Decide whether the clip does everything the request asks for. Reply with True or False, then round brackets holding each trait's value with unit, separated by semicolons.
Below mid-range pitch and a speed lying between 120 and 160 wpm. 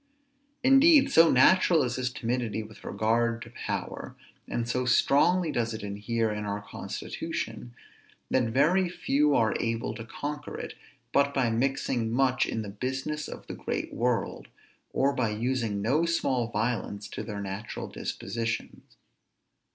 True (120 Hz; 150 wpm)